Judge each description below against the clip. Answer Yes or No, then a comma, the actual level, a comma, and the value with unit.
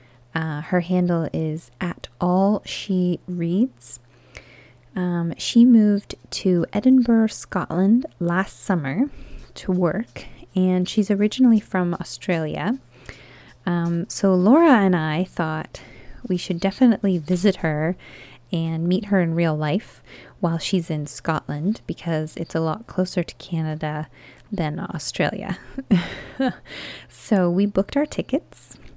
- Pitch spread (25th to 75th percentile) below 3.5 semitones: No, average, 3.8 semitones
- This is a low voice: No, medium, 180 Hz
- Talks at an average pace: No, slow, 120 wpm